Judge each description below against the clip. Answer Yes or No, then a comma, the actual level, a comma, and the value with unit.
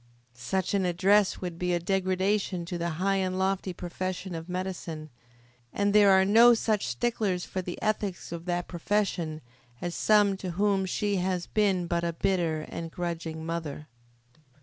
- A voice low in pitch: No, medium, 185 Hz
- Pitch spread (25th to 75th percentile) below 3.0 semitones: Yes, narrow, 2.4 semitones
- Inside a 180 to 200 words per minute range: No, average, 170 wpm